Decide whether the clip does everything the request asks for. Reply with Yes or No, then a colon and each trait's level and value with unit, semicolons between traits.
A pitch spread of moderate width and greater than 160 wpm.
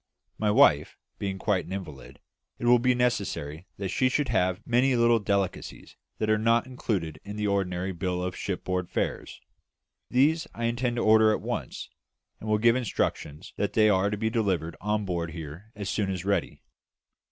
Yes: average, 4.1 semitones; average, 180 wpm